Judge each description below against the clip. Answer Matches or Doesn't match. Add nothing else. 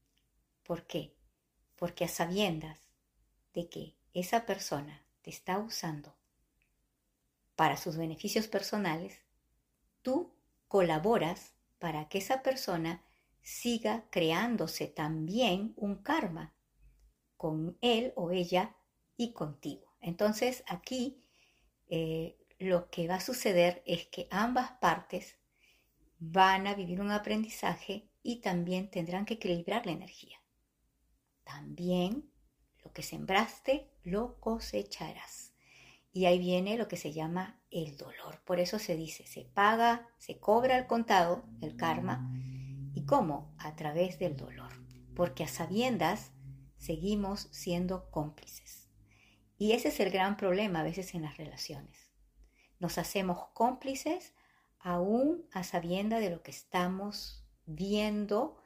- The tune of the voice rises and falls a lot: Doesn't match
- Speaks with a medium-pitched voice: Matches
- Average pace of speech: Doesn't match